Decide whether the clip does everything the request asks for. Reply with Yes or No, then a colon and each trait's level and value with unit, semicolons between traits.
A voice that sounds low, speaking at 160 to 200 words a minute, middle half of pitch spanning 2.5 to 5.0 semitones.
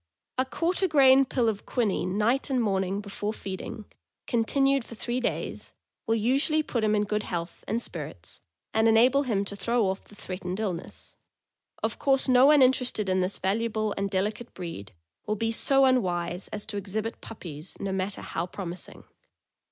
No: high, 215 Hz; average, 170 wpm; average, 4.6 semitones